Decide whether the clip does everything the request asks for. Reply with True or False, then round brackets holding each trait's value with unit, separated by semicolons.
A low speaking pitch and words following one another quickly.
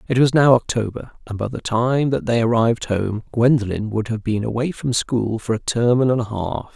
True (115 Hz; 220 wpm)